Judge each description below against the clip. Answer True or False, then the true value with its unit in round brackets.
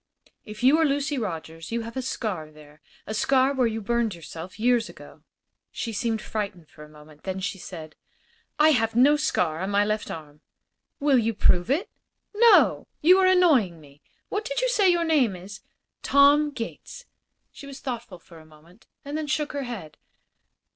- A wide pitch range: True (8.1 semitones)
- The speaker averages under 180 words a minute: False (185 wpm)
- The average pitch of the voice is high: True (225 Hz)